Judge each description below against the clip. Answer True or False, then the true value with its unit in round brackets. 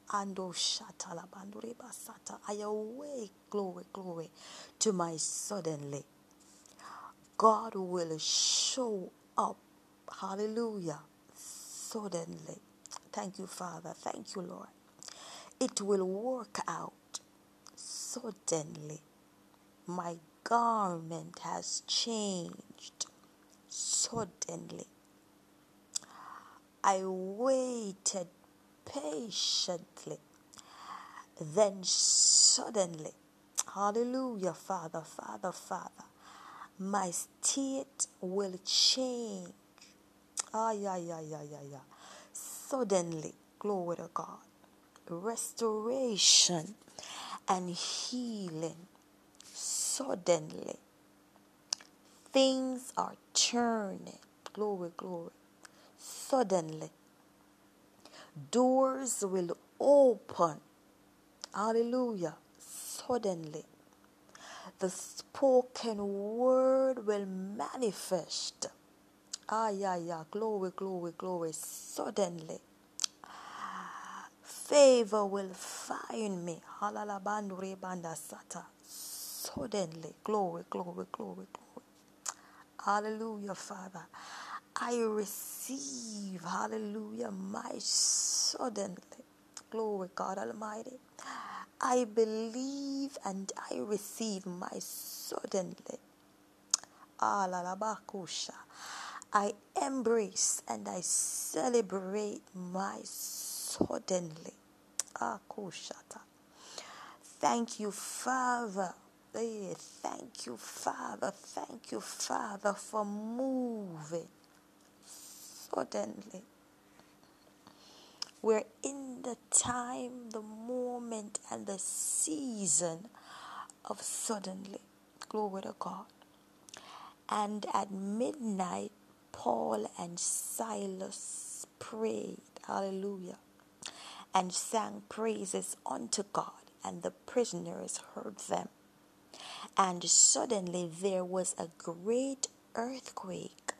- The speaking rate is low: True (70 wpm)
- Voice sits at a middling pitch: False (205 Hz)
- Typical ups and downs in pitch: True (4.5 semitones)